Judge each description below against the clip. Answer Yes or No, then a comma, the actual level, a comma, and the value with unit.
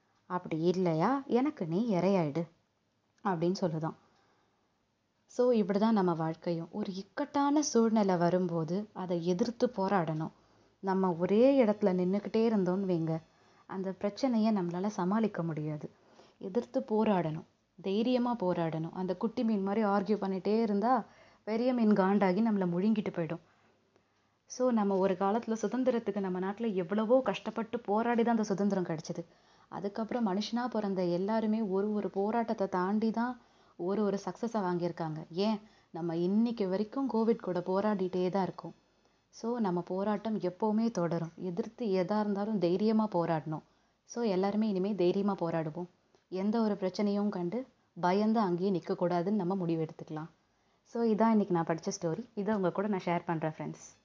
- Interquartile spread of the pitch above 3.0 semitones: Yes, average, 3.7 semitones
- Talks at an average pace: No, fast, 135 wpm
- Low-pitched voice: No, high, 195 Hz